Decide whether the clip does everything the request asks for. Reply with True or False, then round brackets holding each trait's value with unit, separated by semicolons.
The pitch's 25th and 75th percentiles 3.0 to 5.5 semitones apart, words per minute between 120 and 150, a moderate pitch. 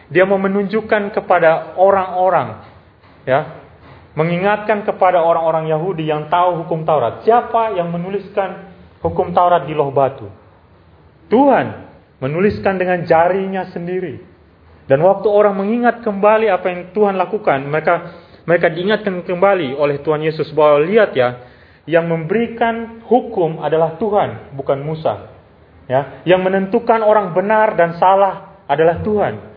True (5.2 semitones; 125 wpm; 175 Hz)